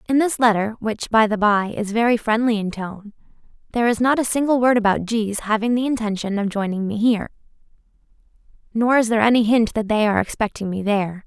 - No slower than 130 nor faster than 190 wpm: No, average, 200 wpm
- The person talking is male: No, female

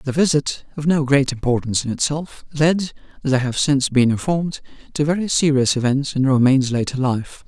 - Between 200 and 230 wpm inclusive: No, average, 170 wpm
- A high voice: No, medium, 140 Hz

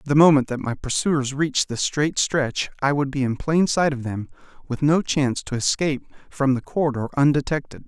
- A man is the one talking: Yes, male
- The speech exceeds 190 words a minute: Yes, average, 200 wpm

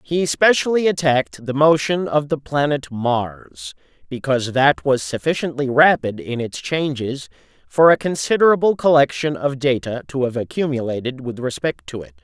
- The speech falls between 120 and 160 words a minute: Yes, average, 145 wpm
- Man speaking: Yes, male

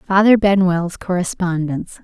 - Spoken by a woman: Yes, female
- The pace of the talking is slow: Yes, slow, 90 wpm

